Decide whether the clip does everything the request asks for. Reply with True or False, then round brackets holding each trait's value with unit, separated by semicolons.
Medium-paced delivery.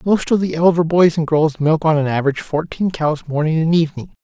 False (225 wpm)